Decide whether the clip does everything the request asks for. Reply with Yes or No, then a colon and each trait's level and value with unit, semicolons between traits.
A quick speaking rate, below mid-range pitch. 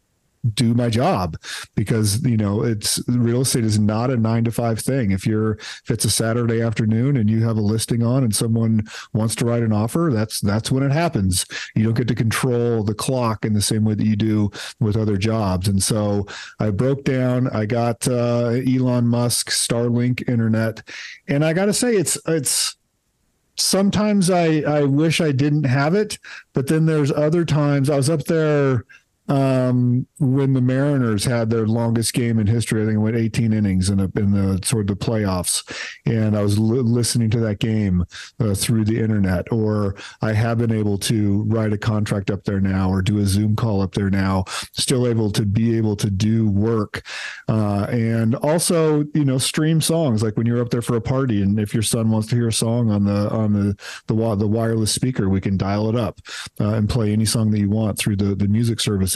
Yes: fast, 210 wpm; low, 115 Hz